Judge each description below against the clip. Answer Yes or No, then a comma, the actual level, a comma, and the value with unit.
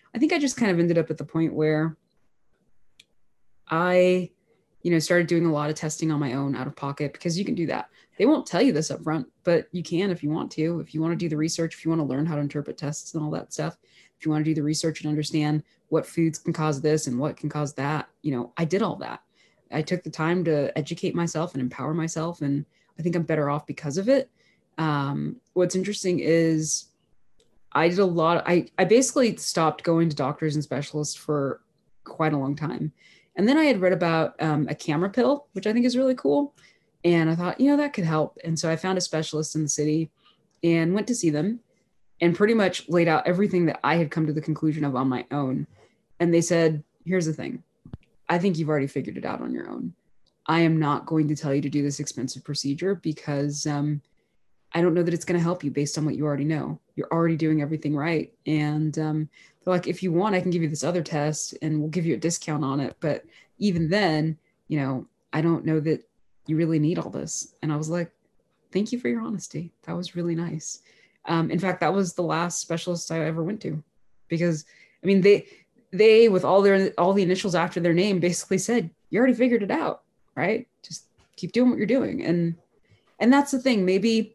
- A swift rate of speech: Yes, fast, 235 wpm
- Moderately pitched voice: Yes, medium, 165 Hz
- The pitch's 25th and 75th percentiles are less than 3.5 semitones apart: Yes, average, 3.1 semitones